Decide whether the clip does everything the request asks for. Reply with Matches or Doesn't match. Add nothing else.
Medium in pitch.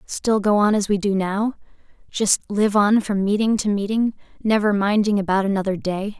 Doesn't match